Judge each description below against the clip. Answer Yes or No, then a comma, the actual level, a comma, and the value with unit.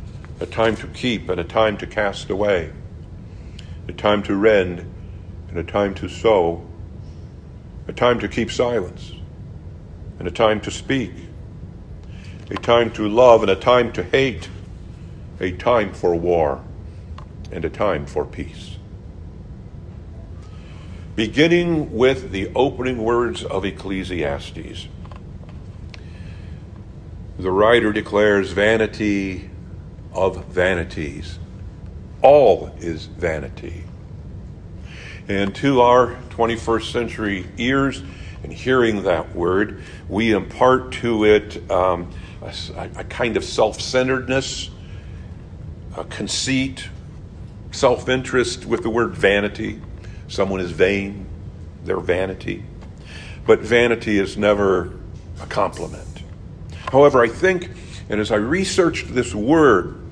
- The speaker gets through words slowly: Yes, slow, 110 wpm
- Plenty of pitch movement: No, average, 3.9 semitones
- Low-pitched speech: Yes, very low, 95 Hz